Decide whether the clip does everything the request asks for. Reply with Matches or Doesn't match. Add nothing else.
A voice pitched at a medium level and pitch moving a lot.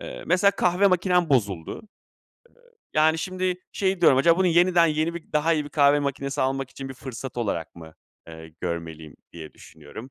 Matches